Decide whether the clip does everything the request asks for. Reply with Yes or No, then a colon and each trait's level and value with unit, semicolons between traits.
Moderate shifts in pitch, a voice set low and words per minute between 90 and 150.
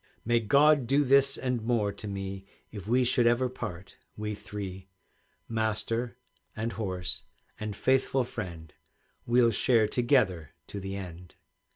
Yes: average, 4.1 semitones; low, 110 Hz; average, 140 wpm